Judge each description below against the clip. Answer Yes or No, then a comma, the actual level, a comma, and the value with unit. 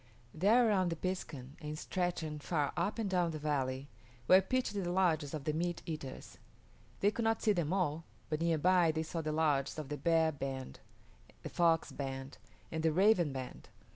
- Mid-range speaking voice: Yes, medium, 160 Hz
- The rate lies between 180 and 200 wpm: Yes, average, 190 wpm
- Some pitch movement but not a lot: Yes, average, 3.7 semitones